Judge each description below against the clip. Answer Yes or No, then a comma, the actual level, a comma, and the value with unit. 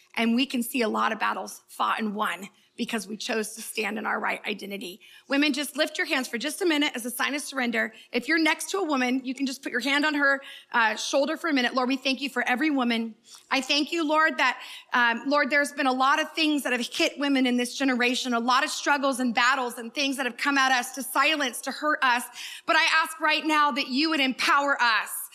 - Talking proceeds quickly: Yes, fast, 255 wpm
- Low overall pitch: No, very high, 270 Hz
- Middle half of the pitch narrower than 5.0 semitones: Yes, average, 3.3 semitones